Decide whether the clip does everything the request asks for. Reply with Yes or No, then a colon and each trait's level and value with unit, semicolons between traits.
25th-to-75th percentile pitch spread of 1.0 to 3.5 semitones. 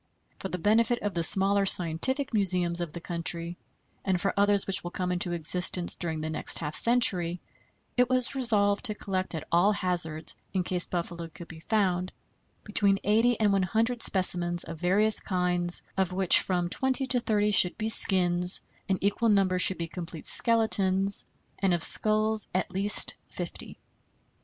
Yes: average, 3.1 semitones